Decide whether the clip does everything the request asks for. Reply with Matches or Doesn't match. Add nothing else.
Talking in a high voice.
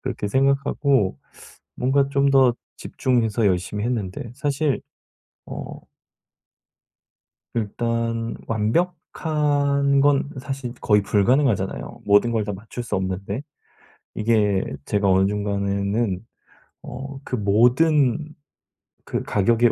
Doesn't match